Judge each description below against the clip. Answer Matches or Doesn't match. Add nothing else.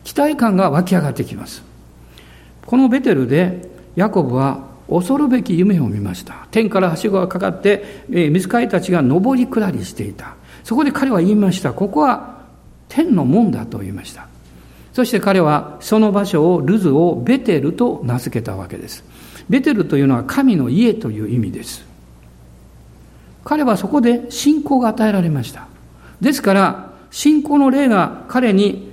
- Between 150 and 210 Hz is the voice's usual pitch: Matches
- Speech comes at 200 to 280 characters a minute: Doesn't match